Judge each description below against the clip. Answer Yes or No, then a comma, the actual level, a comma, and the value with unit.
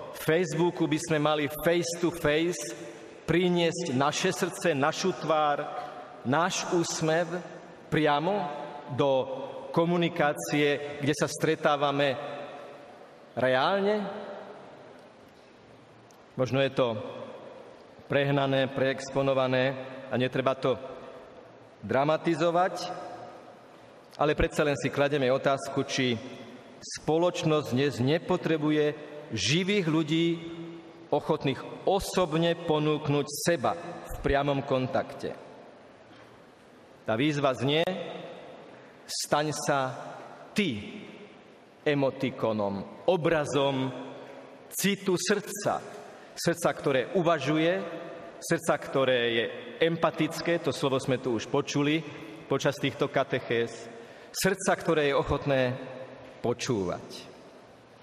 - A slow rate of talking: Yes, slow, 85 wpm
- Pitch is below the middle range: No, medium, 150 Hz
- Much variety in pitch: No, average, 3.8 semitones